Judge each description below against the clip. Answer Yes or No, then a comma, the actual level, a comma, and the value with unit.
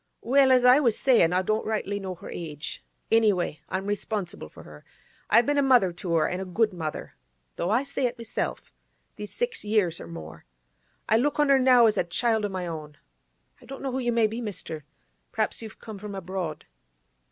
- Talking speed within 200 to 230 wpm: Yes, fast, 205 wpm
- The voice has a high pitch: Yes, high, 210 Hz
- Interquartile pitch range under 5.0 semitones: No, wide, 5.5 semitones